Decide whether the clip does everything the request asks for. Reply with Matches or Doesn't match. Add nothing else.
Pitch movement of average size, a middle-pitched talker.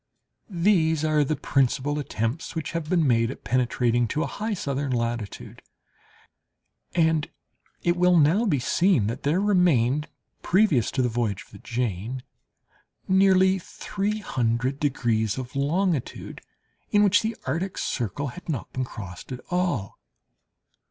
Doesn't match